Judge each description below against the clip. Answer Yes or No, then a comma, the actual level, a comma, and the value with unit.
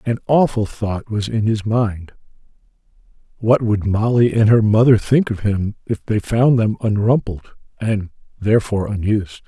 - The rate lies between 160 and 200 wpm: No, average, 150 wpm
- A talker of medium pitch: No, low, 110 Hz